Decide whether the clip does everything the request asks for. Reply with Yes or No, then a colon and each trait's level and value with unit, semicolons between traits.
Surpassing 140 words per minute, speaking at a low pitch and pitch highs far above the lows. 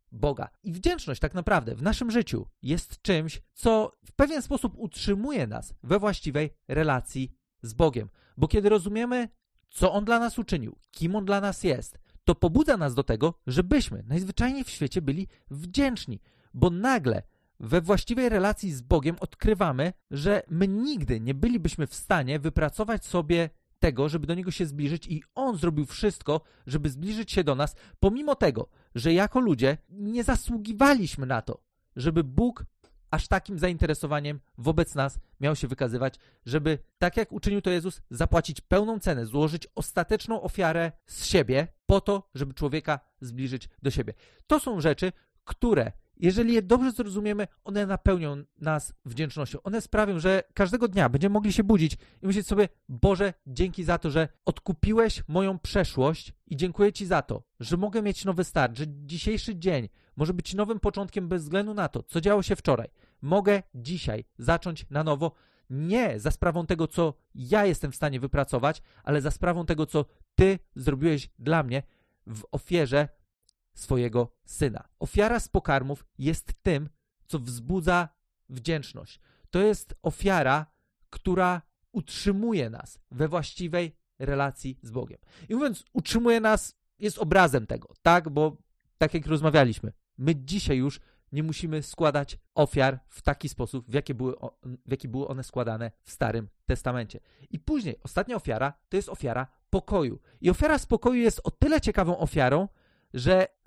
No: average, 155 wpm; medium, 165 Hz; wide, 6.1 semitones